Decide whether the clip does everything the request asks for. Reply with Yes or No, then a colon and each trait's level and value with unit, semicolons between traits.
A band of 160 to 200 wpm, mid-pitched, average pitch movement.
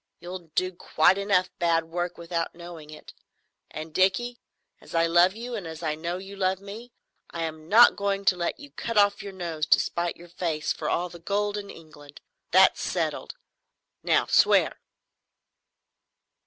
Yes: average, 170 wpm; medium, 175 Hz; average, 3.2 semitones